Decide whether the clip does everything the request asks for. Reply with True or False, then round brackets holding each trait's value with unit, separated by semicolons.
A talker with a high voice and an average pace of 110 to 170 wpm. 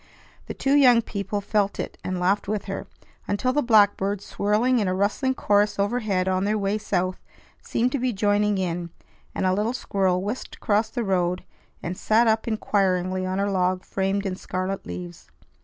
False (200 Hz; 180 wpm)